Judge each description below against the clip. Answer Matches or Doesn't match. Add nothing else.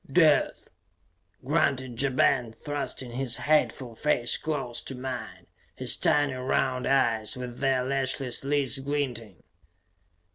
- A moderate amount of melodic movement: Doesn't match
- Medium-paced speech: Doesn't match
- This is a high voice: Doesn't match